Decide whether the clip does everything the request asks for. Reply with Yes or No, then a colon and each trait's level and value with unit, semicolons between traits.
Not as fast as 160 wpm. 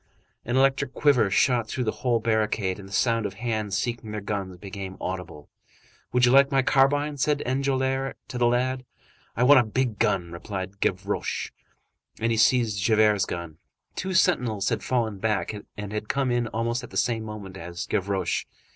No: average, 180 wpm